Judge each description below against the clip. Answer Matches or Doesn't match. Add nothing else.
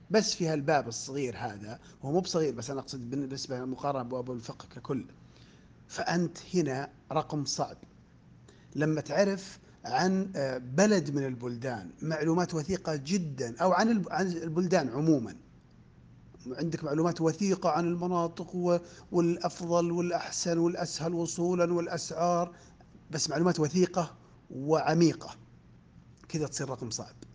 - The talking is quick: Doesn't match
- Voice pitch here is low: Doesn't match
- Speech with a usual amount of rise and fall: Matches